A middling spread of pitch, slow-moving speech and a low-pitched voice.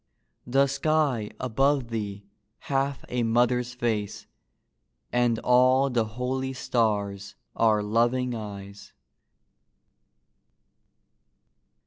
Yes: average, 3.3 semitones; slow, 80 wpm; low, 120 Hz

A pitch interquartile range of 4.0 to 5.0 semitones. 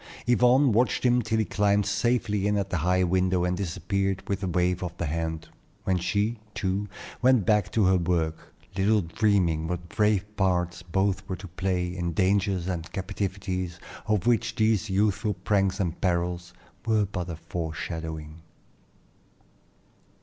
No: average, 2.8 semitones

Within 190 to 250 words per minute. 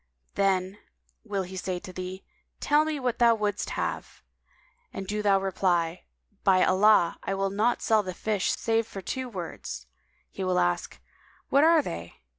No: average, 165 wpm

